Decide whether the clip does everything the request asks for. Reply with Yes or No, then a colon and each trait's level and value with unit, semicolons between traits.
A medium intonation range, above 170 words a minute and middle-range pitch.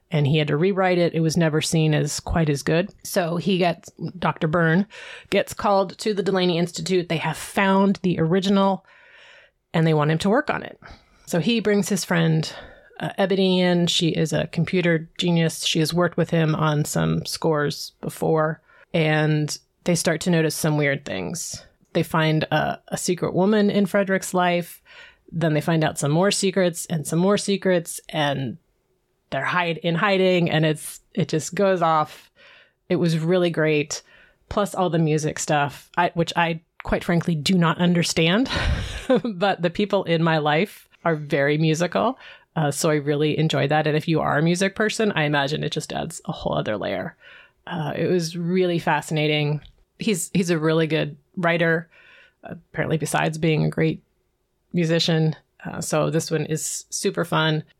Yes: average, 3.0 semitones; average, 180 wpm; medium, 170 Hz